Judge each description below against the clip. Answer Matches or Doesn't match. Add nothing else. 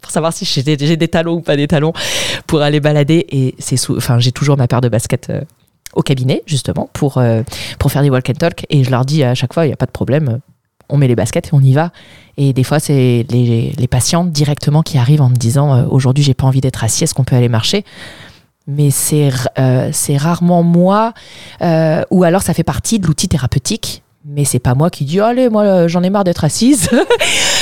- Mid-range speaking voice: Matches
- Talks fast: Matches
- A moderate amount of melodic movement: Matches